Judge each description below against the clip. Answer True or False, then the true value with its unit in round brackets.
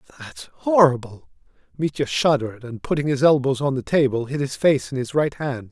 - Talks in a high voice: False (135 Hz)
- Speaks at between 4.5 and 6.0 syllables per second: True (5.4 syllables/s)